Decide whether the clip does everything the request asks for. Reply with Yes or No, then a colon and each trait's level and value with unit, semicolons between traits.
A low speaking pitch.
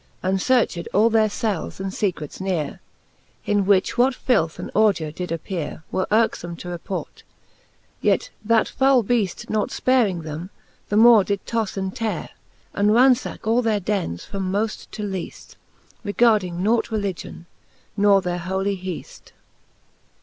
No: high, 200 Hz